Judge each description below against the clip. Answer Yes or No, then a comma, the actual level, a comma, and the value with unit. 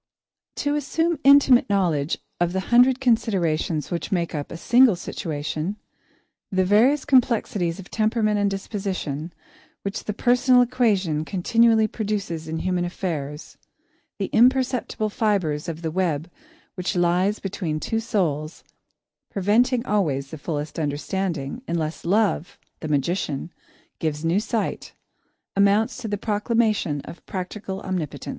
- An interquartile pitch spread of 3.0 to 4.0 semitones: No, average, 5.3 semitones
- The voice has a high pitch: Yes, high, 195 Hz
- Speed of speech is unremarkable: No, slow, 130 wpm